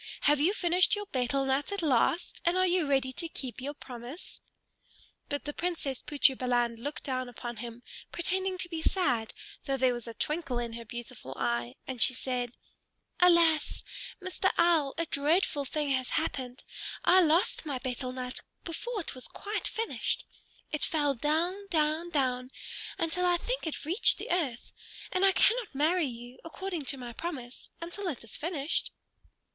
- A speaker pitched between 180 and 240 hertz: No, very high, 290 Hz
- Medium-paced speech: Yes, average, 170 wpm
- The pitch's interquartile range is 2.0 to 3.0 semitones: No, wide, 5.4 semitones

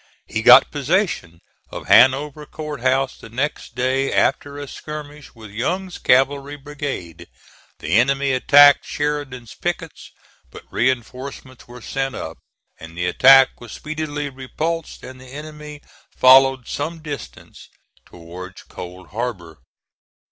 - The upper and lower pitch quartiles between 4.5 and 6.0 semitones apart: No, average, 3.8 semitones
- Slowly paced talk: Yes, slow, 125 wpm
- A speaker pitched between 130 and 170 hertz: Yes, low, 135 Hz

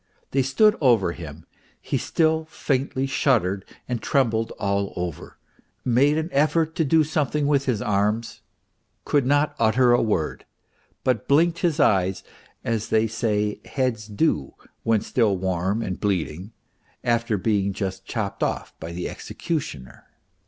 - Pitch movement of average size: No, wide, 5.9 semitones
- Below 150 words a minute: Yes, average, 140 wpm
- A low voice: Yes, low, 115 Hz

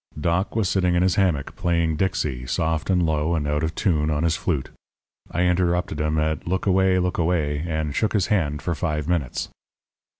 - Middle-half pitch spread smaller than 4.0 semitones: Yes, average, 3.0 semitones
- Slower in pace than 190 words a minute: No, average, 195 wpm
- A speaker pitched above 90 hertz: No, very low, 85 Hz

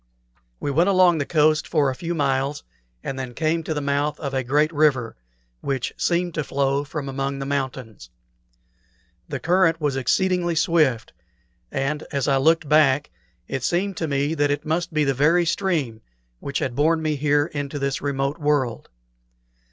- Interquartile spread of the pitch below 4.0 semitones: Yes, average, 2.9 semitones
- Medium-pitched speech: Yes, medium, 145 Hz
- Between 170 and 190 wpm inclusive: Yes, average, 175 wpm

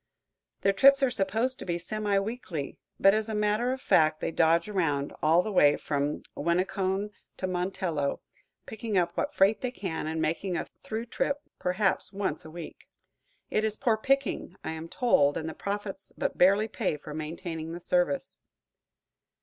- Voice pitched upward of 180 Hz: Yes, high, 190 Hz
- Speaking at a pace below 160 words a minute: No, average, 175 wpm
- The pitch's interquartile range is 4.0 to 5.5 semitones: Yes, average, 4.9 semitones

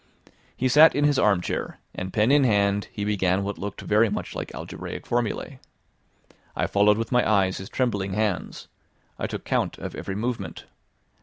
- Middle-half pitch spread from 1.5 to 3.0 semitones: No, average, 3.4 semitones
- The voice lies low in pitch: Yes, low, 105 Hz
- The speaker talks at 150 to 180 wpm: Yes, average, 170 wpm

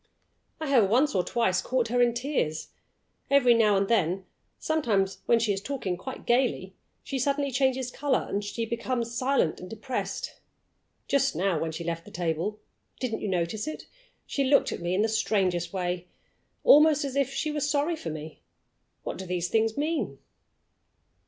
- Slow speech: No, average, 170 wpm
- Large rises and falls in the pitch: Yes, wide, 6.5 semitones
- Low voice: No, high, 230 Hz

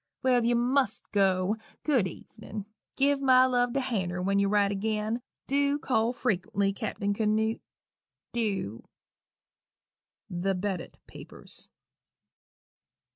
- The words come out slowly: Yes, slow, 115 wpm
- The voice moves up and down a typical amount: Yes, average, 4.1 semitones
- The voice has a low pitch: No, high, 215 Hz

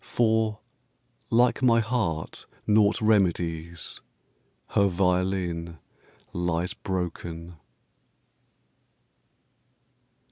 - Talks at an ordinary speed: No, slow, 60 wpm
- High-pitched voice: No, very low, 90 Hz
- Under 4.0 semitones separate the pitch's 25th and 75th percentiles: No, average, 4.3 semitones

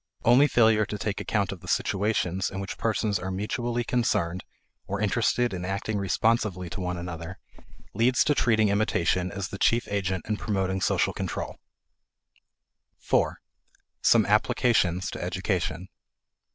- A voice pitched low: Yes, low, 100 Hz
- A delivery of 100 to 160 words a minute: Yes, average, 140 wpm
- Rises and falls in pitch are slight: No, average, 3.2 semitones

